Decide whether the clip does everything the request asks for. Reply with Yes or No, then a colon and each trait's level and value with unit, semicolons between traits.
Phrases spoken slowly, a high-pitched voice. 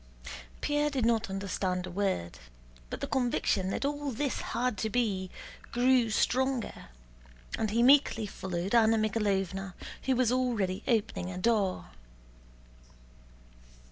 Yes: slow, 125 wpm; high, 220 Hz